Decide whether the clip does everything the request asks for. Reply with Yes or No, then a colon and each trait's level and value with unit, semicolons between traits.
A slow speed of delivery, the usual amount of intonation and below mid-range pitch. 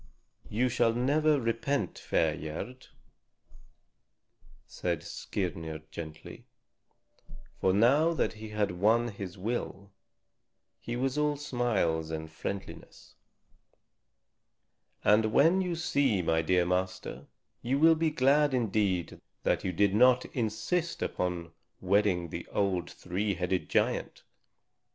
No: slow, 115 wpm; wide, 6.0 semitones; low, 105 Hz